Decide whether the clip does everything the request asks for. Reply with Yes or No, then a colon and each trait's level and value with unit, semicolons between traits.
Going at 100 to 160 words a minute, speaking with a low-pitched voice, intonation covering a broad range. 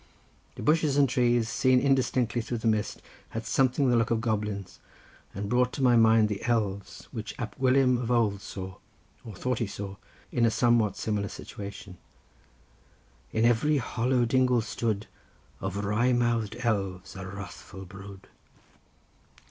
No: average, 150 wpm; low, 115 Hz; average, 3.4 semitones